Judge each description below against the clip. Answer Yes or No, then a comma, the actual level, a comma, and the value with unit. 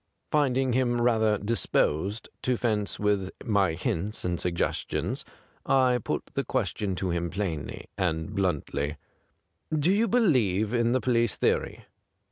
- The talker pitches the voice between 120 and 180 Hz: No, low, 105 Hz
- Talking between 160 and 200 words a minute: No, slow, 135 wpm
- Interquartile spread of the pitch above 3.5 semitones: Yes, average, 5.2 semitones